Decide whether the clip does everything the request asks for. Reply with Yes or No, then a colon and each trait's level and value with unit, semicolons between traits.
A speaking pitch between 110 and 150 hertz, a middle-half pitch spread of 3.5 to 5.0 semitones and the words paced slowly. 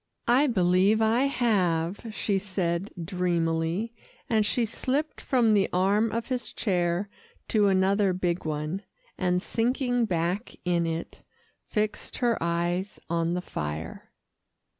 No: high, 190 Hz; average, 4.4 semitones; slow, 125 wpm